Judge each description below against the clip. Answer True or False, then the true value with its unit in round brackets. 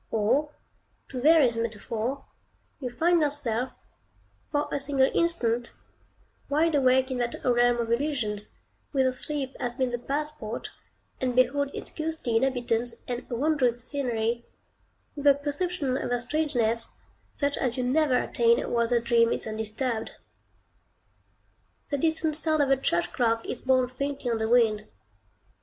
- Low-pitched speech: False (255 Hz)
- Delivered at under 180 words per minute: True (145 wpm)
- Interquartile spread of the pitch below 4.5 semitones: True (3.4 semitones)